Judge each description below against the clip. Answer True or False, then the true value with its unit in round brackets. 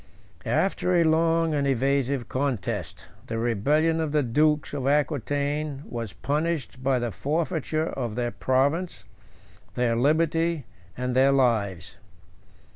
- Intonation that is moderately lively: True (4.1 semitones)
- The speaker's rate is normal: False (120 wpm)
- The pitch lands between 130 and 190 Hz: True (140 Hz)